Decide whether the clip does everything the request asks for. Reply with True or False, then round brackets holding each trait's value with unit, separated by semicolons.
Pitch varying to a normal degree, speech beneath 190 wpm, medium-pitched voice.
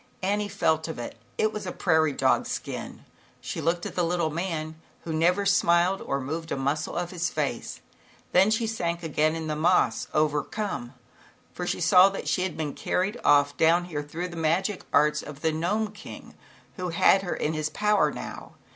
False (3.3 semitones; 195 wpm; 170 Hz)